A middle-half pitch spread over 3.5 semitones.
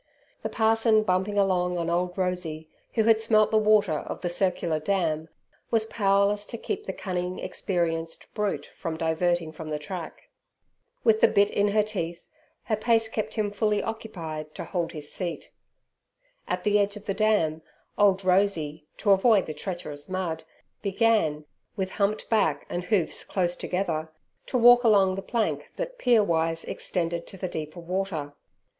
Yes: average, 4.4 semitones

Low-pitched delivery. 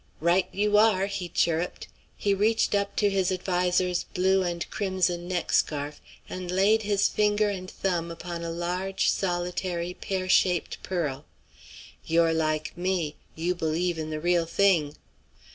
No: medium, 180 Hz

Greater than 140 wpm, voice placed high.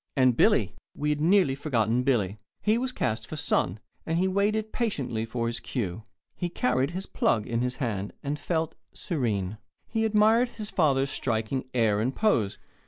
No: average, 170 wpm; low, 135 Hz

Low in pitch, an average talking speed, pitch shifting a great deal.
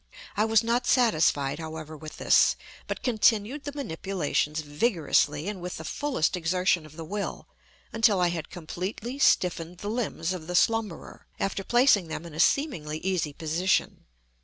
No: medium, 180 Hz; average, 160 wpm; wide, 5.7 semitones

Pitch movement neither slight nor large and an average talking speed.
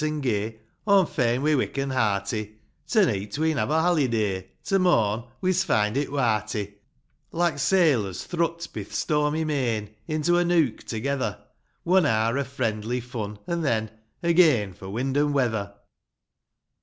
No: wide, 6.6 semitones; average, 155 wpm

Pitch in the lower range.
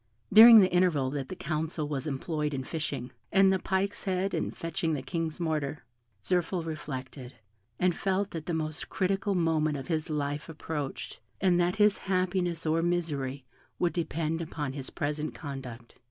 No: medium, 160 Hz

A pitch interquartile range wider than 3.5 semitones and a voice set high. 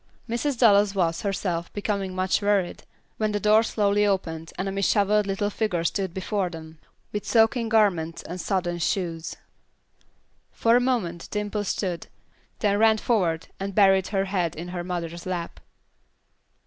No: average, 3.1 semitones; high, 195 Hz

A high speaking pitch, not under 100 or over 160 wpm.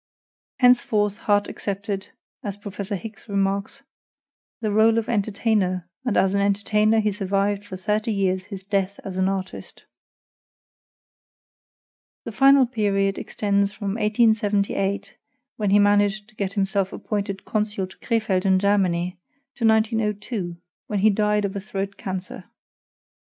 Yes: high, 205 Hz; slow, 135 wpm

